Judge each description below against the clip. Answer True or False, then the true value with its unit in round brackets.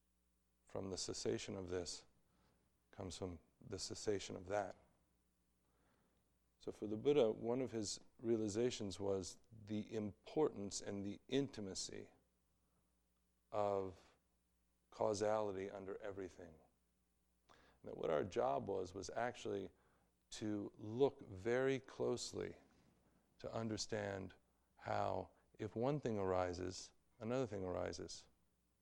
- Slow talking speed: True (105 wpm)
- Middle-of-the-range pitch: False (95 Hz)